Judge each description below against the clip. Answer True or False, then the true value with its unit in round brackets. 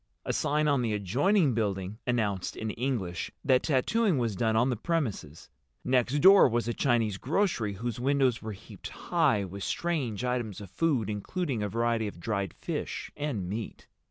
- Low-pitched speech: True (120 Hz)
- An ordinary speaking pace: True (160 wpm)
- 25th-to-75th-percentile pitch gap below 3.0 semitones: False (5.0 semitones)